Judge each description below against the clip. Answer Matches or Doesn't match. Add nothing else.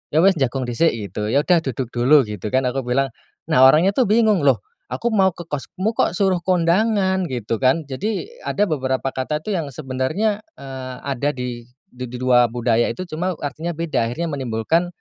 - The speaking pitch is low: Doesn't match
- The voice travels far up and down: Matches